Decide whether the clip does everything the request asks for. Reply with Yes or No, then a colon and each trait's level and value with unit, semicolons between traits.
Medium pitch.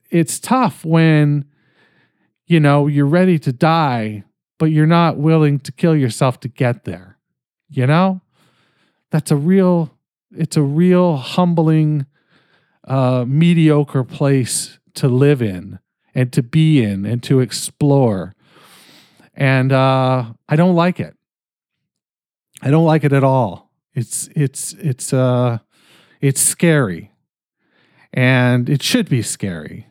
Yes: medium, 145 Hz